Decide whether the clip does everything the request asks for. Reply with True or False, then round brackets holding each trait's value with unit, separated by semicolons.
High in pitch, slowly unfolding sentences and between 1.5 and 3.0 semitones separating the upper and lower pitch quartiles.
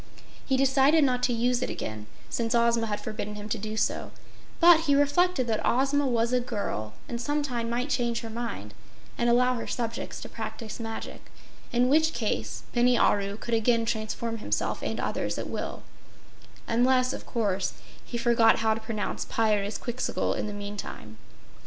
False (235 Hz; 170 wpm; 2.6 semitones)